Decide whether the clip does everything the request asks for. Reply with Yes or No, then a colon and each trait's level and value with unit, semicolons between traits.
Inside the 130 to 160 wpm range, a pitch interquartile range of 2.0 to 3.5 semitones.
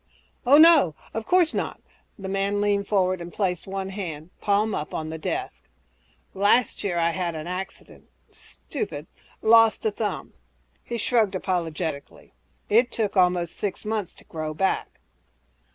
No: average, 150 wpm; average, 3.9 semitones